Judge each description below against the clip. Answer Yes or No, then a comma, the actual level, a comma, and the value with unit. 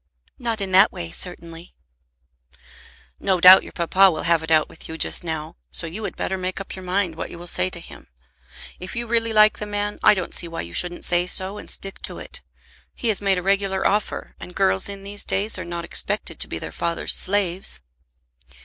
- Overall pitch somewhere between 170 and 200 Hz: Yes, medium, 185 Hz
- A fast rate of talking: Yes, fast, 220 wpm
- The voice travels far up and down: No, average, 3.0 semitones